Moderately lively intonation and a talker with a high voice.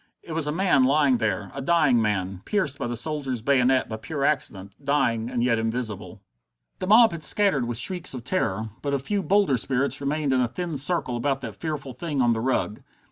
No: average, 4.6 semitones; low, 135 Hz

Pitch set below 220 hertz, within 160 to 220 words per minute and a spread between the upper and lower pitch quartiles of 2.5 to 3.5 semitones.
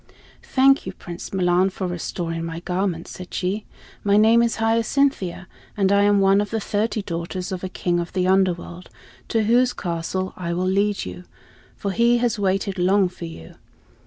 Yes: high, 190 Hz; average, 180 wpm; average, 2.9 semitones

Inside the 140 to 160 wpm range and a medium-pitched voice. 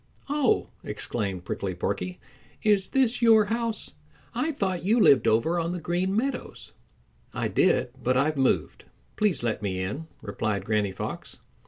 Yes: average, 150 wpm; medium, 165 Hz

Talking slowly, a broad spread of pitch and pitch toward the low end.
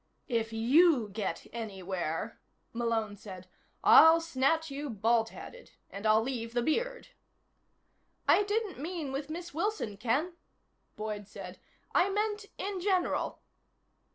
No: slow, 120 wpm; wide, 8.0 semitones; very high, 260 Hz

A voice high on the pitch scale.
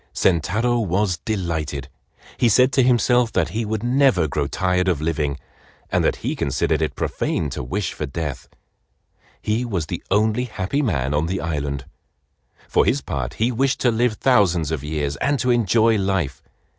No: very low, 95 Hz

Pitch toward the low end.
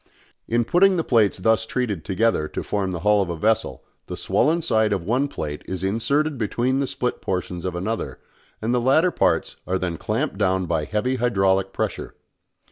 Yes: low, 105 Hz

